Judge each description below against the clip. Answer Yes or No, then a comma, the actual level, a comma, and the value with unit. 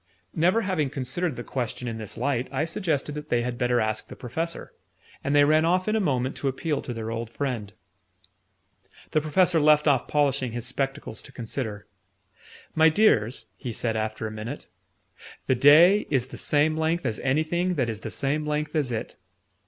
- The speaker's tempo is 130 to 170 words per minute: No, average, 185 wpm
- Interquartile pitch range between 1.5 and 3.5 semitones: No, average, 4.6 semitones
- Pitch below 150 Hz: Yes, medium, 140 Hz